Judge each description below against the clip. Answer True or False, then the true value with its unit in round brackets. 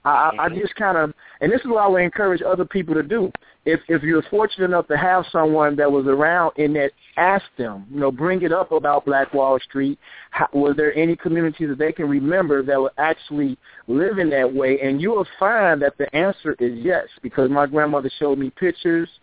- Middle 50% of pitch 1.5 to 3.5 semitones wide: False (3.9 semitones)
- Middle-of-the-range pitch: True (155 Hz)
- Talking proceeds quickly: True (220 wpm)